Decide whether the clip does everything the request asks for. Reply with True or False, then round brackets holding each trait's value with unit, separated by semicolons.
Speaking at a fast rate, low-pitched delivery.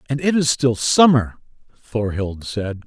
False (145 wpm; 120 Hz)